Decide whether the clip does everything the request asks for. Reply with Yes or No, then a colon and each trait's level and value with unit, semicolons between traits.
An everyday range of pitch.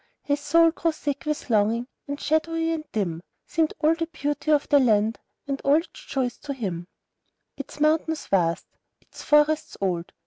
No: wide, 5.9 semitones